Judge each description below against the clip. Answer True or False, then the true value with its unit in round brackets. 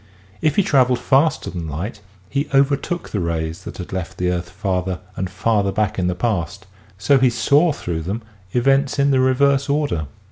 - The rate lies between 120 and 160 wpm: False (185 wpm)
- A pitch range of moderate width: False (7.3 semitones)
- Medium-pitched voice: False (105 Hz)